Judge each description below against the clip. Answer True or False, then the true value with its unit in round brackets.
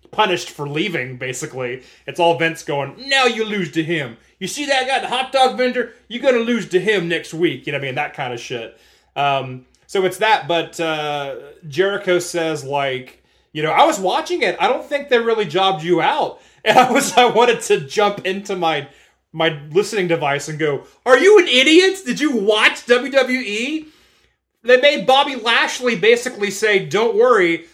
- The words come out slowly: False (195 wpm)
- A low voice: False (205 Hz)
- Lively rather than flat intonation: True (7.8 semitones)